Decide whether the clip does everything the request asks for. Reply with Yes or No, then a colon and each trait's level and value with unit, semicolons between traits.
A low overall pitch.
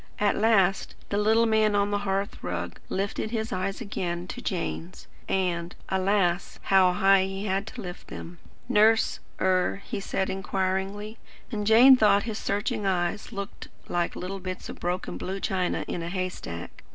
No: high, 195 Hz